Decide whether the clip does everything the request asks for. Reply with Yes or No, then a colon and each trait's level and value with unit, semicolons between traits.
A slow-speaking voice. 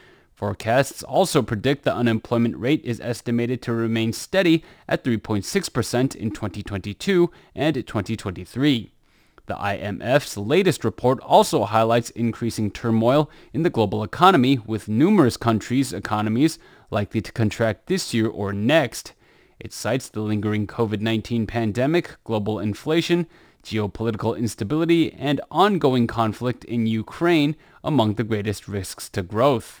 Yes: slow, 125 wpm